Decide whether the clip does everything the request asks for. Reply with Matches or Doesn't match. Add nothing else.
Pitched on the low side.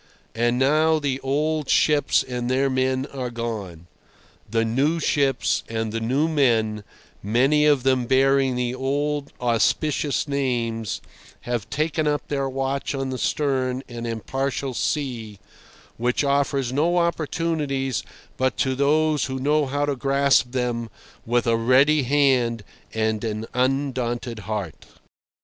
Matches